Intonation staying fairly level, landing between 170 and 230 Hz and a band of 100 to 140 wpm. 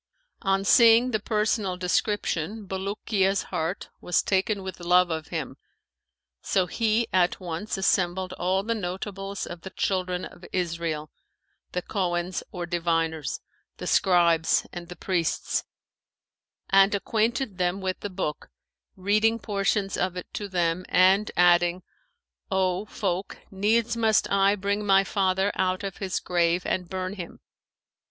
Yes: narrow, 2.3 semitones; high, 190 Hz; slow, 135 wpm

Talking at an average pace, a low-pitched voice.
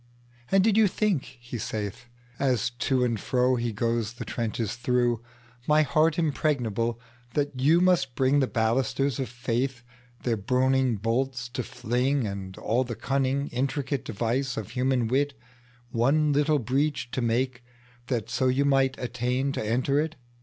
No: slow, 130 wpm; low, 125 Hz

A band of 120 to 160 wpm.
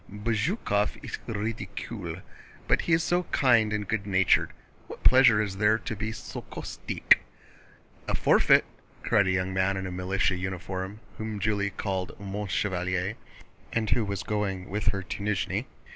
Yes: average, 155 wpm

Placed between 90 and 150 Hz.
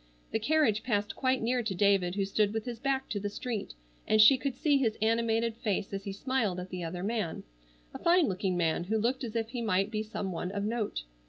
No: high, 215 Hz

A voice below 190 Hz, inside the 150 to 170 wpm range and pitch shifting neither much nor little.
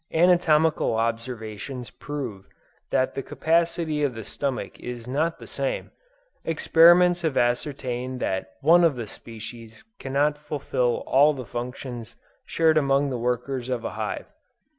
No: low, 135 Hz; slow, 135 wpm; average, 4.4 semitones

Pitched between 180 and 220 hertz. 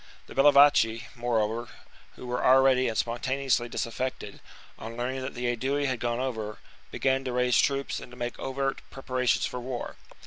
No: low, 125 Hz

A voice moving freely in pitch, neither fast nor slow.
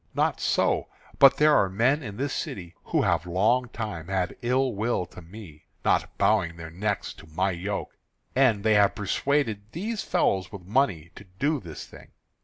Yes: wide, 6.0 semitones; average, 180 wpm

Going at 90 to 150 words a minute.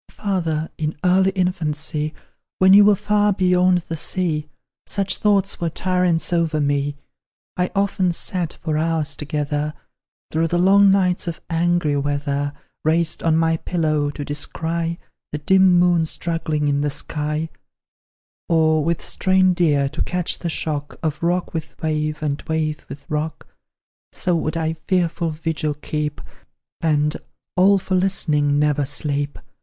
Yes: average, 145 wpm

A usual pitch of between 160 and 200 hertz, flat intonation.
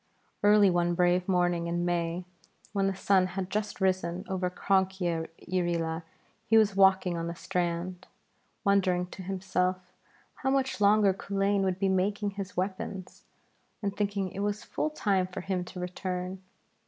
Yes: medium, 185 Hz; narrow, 1.9 semitones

